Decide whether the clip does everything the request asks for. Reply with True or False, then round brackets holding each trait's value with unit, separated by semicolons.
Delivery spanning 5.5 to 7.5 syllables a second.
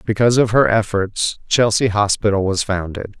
False (5.1 syllables/s)